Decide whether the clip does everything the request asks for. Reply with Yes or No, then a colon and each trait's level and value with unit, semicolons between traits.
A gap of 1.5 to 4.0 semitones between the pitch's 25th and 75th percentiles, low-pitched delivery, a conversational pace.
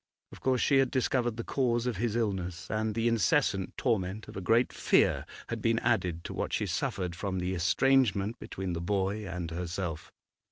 No: average, 4.6 semitones; low, 100 Hz; average, 190 wpm